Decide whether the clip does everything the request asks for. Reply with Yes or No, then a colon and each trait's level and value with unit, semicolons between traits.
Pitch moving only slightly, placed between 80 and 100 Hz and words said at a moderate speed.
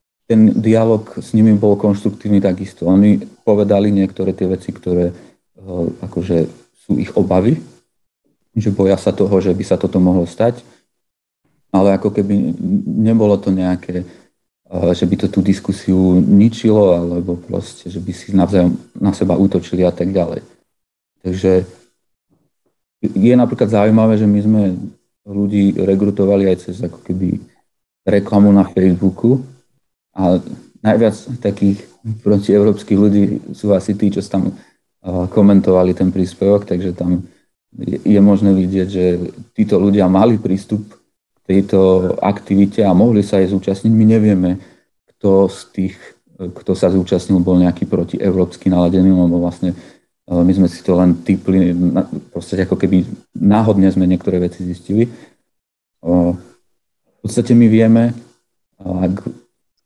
Yes: narrow, 2.2 semitones; very low, 95 Hz; average, 130 wpm